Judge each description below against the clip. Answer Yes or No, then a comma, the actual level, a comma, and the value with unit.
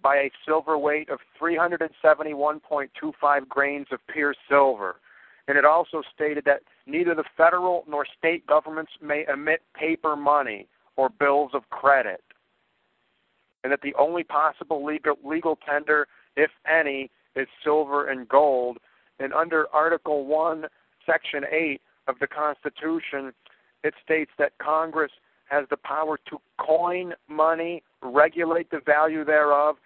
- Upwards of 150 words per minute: No, slow, 135 wpm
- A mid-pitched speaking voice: Yes, medium, 150 Hz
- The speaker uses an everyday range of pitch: No, narrow, 1.8 semitones